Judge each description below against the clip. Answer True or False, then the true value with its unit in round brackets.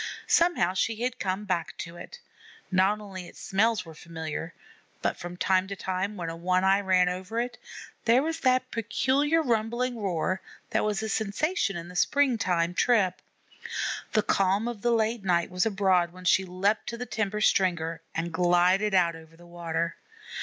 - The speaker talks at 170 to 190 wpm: True (180 wpm)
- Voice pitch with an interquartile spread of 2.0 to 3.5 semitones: False (4.2 semitones)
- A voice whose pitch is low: False (190 Hz)